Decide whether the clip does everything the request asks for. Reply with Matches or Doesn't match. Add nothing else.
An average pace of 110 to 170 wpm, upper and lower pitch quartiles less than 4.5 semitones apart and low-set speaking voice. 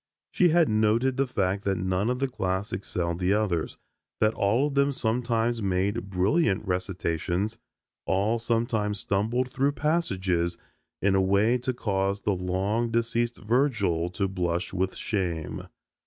Matches